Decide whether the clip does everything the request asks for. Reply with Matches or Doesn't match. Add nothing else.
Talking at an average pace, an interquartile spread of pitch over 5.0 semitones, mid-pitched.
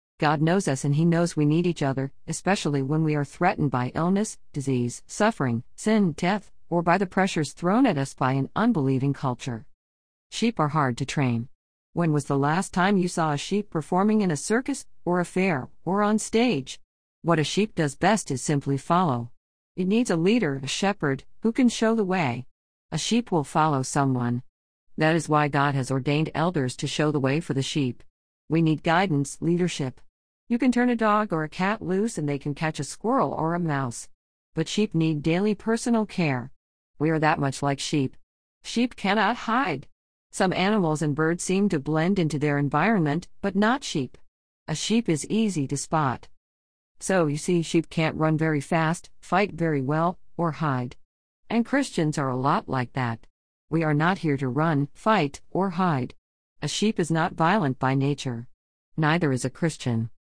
Matches